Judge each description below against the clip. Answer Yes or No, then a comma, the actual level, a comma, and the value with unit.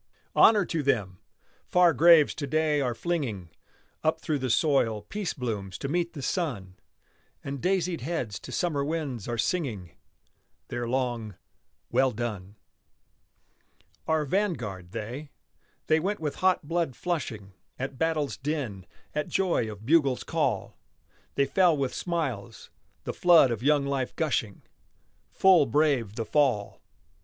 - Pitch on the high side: No, medium, 140 Hz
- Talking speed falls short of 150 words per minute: Yes, slow, 135 wpm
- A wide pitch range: Yes, wide, 6.1 semitones